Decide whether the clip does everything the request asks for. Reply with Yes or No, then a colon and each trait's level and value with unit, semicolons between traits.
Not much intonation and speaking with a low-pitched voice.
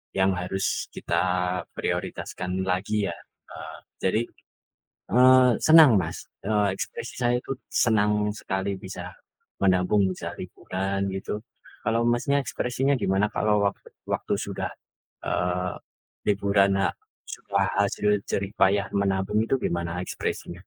Yes: narrow, 2.1 semitones; low, 100 Hz